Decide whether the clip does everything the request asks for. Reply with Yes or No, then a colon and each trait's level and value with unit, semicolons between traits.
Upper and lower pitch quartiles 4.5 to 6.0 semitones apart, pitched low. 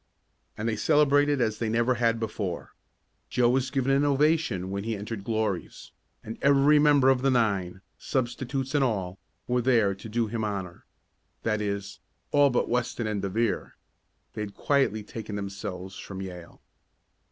Yes: average, 4.8 semitones; low, 115 Hz